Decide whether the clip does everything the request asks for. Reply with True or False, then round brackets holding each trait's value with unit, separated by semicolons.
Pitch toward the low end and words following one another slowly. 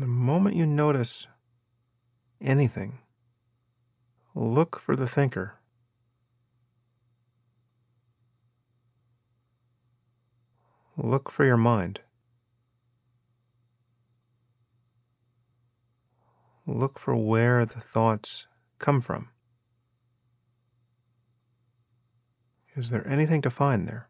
True (120 Hz; 65 wpm)